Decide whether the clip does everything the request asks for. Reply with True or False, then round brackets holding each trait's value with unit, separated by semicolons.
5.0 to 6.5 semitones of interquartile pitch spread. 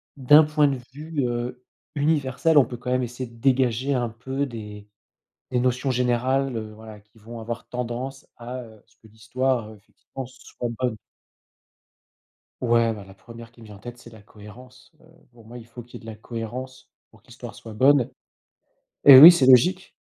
False (2.6 semitones)